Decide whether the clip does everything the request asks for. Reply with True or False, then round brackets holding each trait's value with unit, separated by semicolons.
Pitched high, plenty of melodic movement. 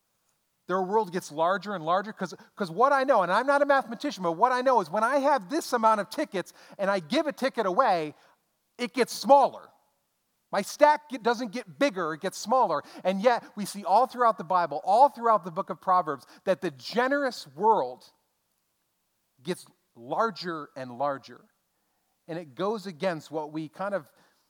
True (200 Hz; 6.1 semitones)